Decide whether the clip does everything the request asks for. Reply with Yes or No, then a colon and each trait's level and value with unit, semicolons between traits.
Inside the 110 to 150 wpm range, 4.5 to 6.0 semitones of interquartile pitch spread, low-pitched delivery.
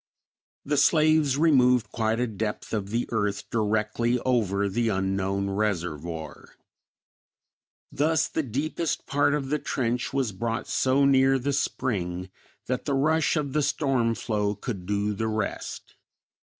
Yes: slow, 135 wpm; average, 5.2 semitones; low, 115 Hz